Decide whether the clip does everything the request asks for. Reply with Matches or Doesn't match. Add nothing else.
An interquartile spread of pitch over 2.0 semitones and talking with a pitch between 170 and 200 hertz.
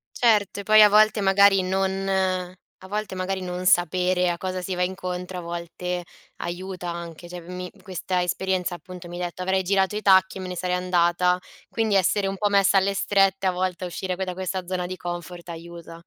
Doesn't match